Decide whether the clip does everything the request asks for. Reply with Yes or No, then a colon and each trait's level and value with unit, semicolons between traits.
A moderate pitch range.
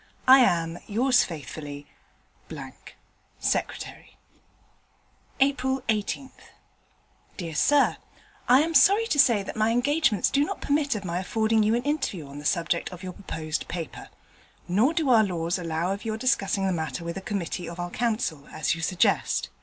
No: wide, 7.2 semitones